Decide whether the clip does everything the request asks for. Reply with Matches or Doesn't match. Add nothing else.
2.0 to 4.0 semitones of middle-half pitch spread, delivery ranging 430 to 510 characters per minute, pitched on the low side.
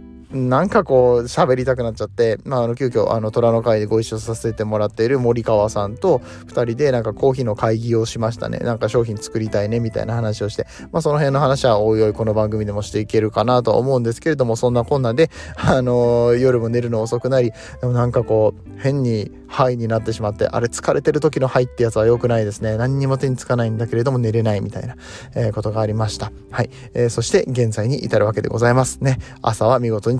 Matches